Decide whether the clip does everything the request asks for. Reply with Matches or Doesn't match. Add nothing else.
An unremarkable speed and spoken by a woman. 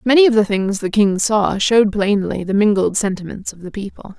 Doesn't match